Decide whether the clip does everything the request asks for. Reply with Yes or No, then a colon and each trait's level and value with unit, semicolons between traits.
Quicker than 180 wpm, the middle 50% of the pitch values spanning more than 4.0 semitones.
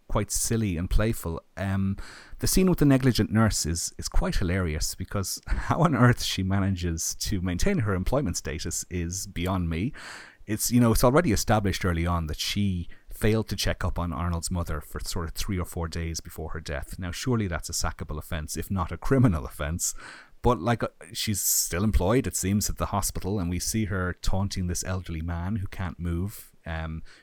No: average, 200 wpm; average, 3.7 semitones